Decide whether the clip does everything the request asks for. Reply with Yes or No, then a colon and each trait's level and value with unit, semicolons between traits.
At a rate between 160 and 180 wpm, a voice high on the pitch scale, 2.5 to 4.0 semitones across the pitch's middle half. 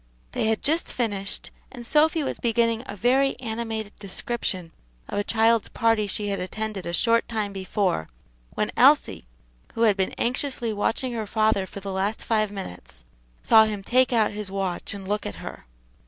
Yes: average, 175 wpm; high, 215 Hz; average, 2.8 semitones